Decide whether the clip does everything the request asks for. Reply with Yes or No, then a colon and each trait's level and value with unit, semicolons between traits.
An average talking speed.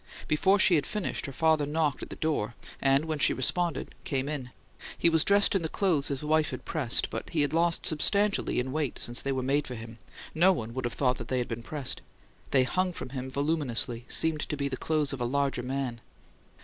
No: fast, 225 wpm